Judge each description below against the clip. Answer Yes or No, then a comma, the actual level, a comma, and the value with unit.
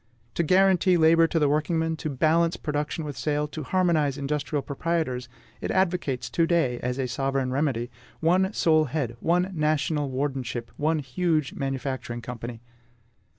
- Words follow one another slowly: No, average, 150 wpm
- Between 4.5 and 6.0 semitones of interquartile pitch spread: No, average, 3.8 semitones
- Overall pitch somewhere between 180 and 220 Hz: No, medium, 150 Hz